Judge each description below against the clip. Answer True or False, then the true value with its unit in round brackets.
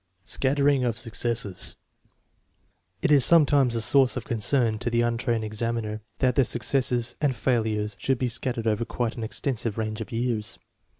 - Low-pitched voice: True (120 Hz)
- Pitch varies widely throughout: False (2.8 semitones)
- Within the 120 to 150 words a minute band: False (170 wpm)